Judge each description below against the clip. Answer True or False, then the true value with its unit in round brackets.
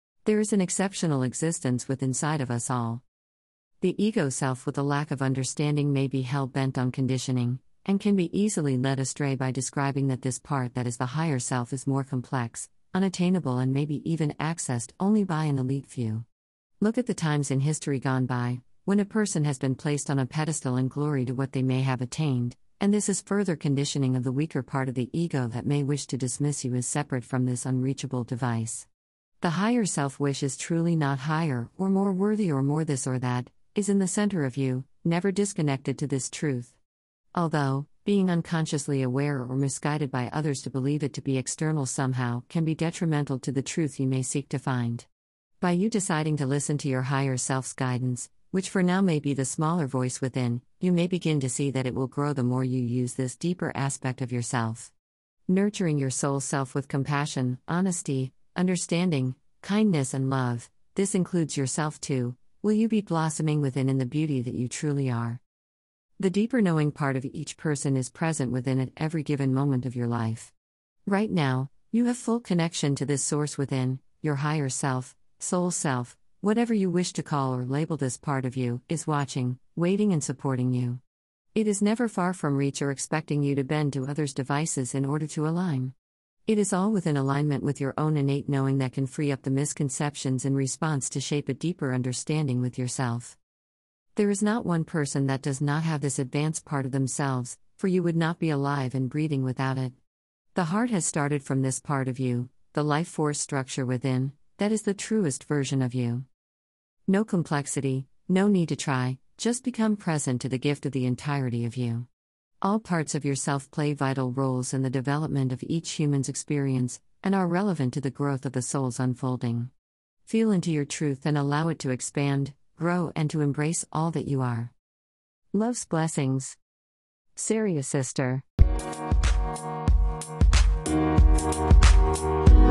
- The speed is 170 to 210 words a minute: True (190 wpm)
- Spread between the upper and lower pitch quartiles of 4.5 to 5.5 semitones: False (3.6 semitones)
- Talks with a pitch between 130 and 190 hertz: True (140 Hz)